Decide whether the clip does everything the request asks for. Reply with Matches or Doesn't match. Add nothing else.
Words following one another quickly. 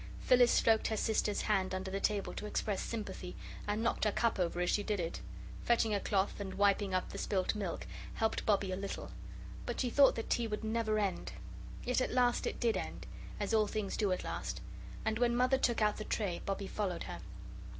Matches